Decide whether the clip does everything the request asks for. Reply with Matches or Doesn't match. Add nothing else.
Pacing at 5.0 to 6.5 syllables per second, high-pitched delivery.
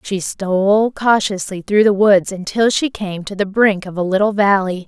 Doesn't match